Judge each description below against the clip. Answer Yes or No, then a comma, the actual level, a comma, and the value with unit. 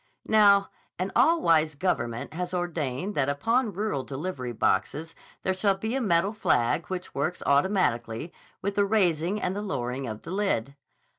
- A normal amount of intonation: No, wide, 6.1 semitones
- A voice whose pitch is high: No, medium, 175 Hz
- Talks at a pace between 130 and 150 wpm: No, average, 160 wpm